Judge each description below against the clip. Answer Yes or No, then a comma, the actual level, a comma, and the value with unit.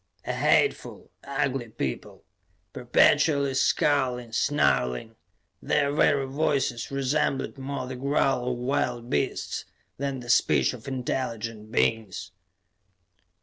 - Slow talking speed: Yes, slow, 105 wpm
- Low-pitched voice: Yes, low, 130 Hz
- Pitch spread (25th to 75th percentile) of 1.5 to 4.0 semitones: Yes, average, 2.8 semitones